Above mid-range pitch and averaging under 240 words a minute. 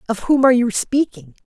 Yes: high, 235 Hz; fast, 205 wpm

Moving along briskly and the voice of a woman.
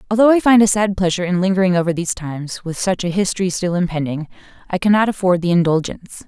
Yes: fast, 210 wpm; female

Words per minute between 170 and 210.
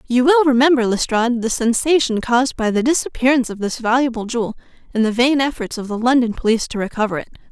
Yes: average, 200 wpm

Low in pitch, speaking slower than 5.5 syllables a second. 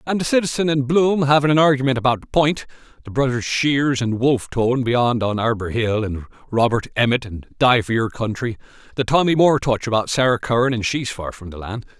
No: low, 125 Hz; 5.7 syllables/s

